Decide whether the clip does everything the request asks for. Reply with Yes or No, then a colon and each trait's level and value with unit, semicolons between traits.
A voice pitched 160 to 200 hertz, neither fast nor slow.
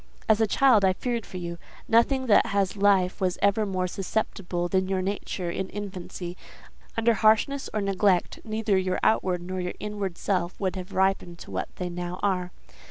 Yes: high, 190 Hz; average, 180 wpm